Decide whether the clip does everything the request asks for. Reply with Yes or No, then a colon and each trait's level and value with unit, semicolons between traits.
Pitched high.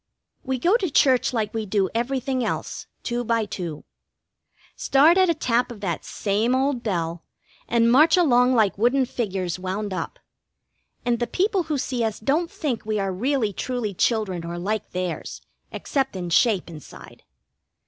Yes: high, 230 Hz